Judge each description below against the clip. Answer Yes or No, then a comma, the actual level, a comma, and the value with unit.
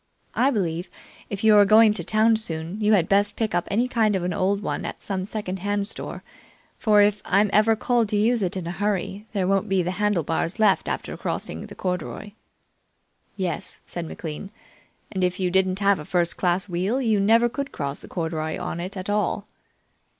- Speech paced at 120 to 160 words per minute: No, average, 200 wpm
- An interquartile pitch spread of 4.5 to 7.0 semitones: No, average, 2.9 semitones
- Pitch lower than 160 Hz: No, high, 195 Hz